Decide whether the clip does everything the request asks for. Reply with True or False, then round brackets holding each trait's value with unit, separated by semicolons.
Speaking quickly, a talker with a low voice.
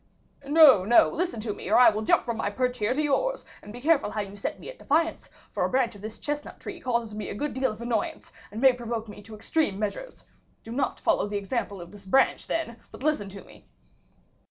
False (240 wpm; 235 Hz)